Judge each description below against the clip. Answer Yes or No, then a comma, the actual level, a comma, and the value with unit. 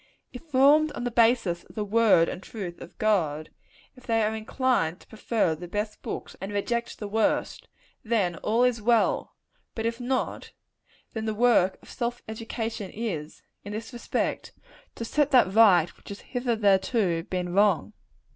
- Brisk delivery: No, average, 165 wpm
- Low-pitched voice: No, high, 220 Hz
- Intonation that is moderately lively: Yes, average, 3.6 semitones